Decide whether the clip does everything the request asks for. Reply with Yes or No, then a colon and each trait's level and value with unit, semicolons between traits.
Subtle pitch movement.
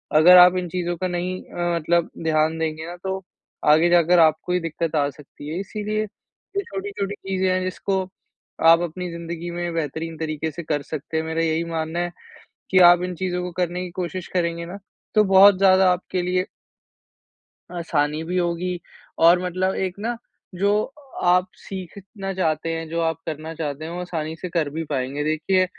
Yes: narrow, 2.3 semitones